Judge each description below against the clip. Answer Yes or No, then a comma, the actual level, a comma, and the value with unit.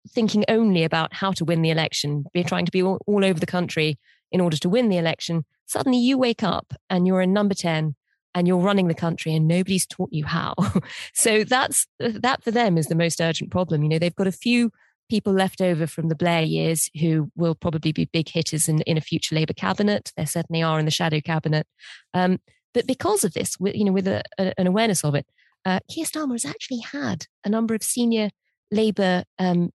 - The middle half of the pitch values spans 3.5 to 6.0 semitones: Yes, average, 4.2 semitones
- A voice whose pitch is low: No, medium, 180 Hz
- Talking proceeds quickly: Yes, fast, 220 wpm